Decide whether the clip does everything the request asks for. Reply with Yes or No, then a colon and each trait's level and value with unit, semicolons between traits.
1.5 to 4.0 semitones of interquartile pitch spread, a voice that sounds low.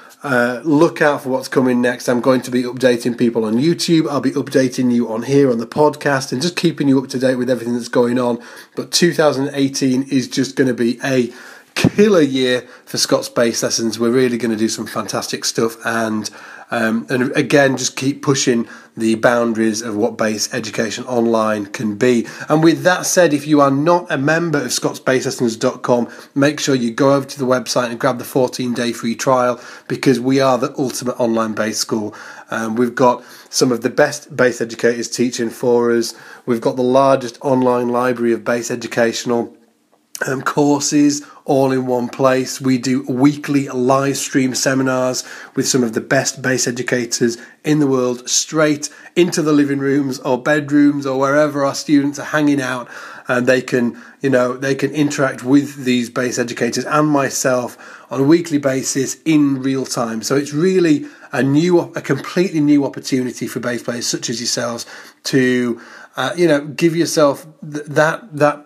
Yes: average, 2.8 semitones; low, 130 Hz